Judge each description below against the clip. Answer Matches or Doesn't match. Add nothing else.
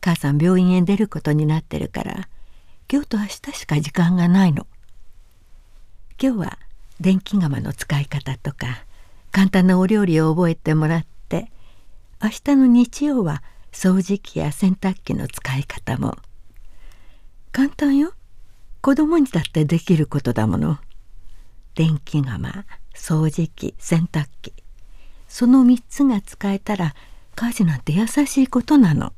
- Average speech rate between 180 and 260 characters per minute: Matches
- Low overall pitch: Doesn't match